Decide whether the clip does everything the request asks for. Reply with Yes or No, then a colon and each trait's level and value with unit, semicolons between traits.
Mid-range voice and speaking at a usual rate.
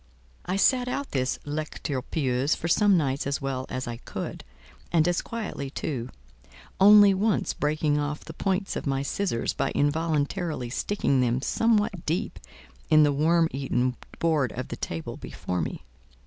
Yes: medium, 150 Hz; average, 160 wpm